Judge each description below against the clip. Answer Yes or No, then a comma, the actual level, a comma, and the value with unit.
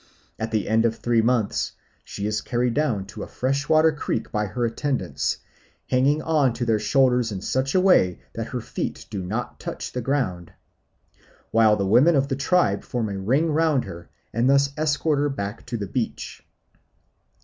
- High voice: No, low, 125 Hz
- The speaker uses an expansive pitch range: No, average, 4.8 semitones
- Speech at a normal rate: Yes, average, 180 wpm